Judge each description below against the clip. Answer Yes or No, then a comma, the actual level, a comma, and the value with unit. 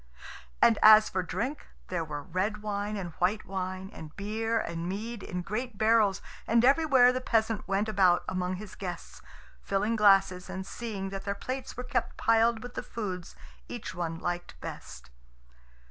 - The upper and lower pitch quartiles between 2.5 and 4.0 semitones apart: Yes, average, 3.5 semitones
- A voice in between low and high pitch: No, high, 200 Hz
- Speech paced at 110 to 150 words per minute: No, average, 165 wpm